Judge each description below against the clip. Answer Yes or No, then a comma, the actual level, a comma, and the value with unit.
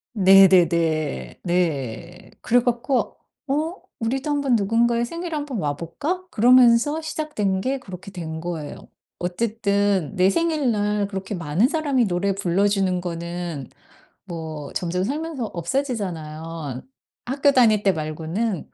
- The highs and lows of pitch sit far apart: Yes, wide, 6.5 semitones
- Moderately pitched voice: No, high, 200 Hz